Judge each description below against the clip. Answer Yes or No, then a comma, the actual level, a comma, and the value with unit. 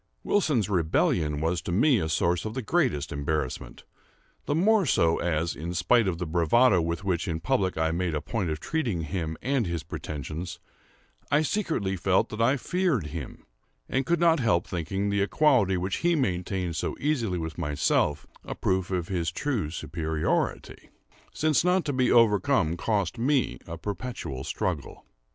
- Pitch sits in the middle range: No, very low, 95 Hz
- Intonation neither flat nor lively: No, wide, 7.7 semitones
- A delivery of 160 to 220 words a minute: Yes, average, 170 wpm